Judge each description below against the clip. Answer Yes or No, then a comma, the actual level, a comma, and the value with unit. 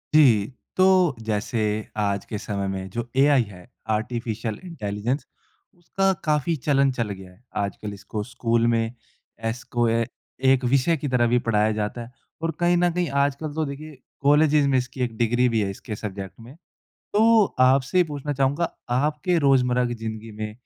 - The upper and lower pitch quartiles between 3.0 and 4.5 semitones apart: No, average, 5.2 semitones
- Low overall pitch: Yes, low, 125 Hz